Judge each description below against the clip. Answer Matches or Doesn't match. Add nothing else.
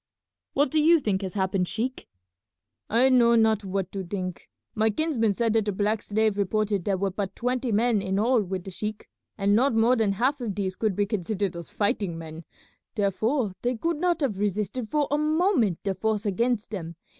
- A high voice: Matches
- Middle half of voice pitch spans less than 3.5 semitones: Doesn't match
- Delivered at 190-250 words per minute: Matches